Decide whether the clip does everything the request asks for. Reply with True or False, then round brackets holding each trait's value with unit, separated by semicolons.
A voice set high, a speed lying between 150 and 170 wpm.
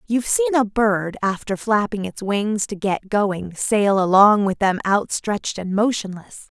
True (200 Hz; 165 wpm)